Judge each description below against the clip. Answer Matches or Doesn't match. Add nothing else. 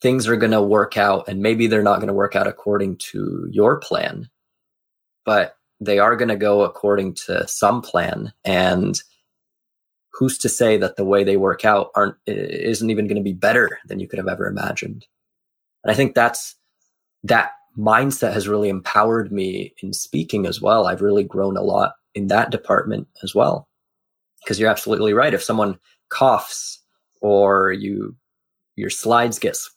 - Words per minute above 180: Doesn't match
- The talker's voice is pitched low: Matches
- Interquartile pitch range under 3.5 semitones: Matches